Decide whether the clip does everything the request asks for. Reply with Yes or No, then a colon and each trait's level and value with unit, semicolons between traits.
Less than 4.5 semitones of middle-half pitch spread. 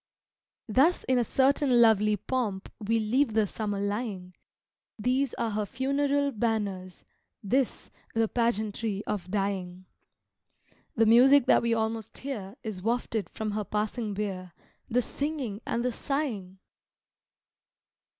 Yes: average, 3.6 semitones